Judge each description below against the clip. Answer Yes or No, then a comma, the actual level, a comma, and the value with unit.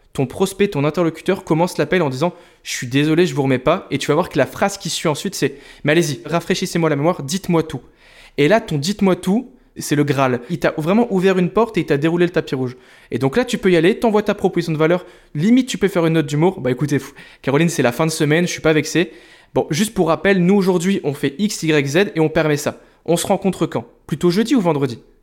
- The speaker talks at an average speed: No, fast, 255 wpm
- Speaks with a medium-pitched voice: Yes, medium, 170 Hz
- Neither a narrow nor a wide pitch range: Yes, average, 4.2 semitones